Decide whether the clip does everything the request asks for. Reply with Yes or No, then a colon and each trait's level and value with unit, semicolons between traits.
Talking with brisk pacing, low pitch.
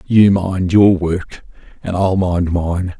No: average, 160 wpm; very low, 90 Hz